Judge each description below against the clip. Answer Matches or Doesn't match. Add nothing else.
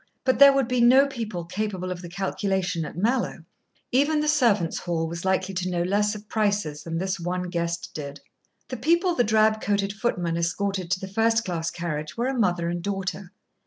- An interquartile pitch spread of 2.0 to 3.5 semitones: Doesn't match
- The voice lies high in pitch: Matches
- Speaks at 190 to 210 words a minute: Matches